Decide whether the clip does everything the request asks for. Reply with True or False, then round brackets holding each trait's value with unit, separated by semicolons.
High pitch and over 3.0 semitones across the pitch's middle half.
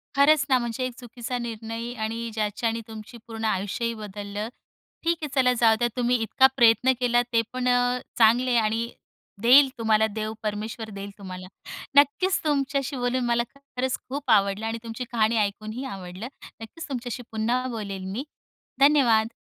False (235 Hz; 2.6 semitones)